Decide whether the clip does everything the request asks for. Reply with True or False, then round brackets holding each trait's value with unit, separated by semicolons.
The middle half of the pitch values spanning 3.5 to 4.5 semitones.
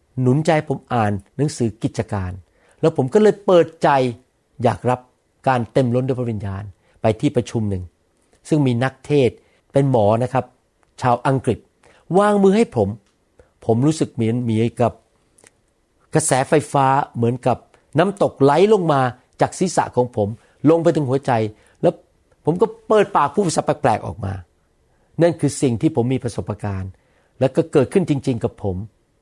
False (5.0 semitones)